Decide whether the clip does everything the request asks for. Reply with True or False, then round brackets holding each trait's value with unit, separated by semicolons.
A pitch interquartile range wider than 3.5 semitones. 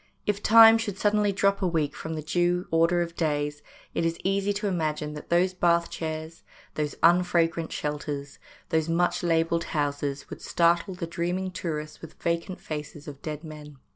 False (2.8 semitones)